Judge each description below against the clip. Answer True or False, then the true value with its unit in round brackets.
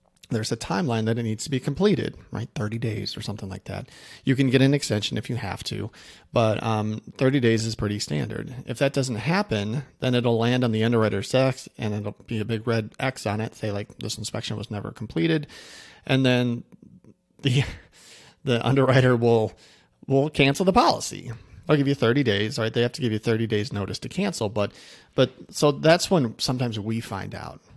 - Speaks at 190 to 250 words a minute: True (205 wpm)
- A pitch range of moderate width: True (3.8 semitones)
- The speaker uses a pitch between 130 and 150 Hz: False (115 Hz)